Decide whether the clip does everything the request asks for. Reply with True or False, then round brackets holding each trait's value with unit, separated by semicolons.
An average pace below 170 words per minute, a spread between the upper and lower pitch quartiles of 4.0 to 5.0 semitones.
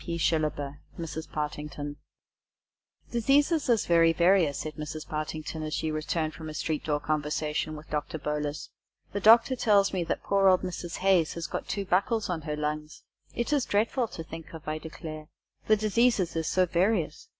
False (185 wpm; 4.3 semitones)